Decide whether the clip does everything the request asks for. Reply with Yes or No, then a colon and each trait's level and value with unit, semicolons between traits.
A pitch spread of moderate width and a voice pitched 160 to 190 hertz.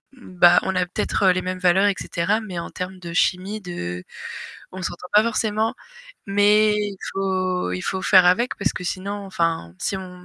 No: narrow, 2.2 semitones; medium, 185 Hz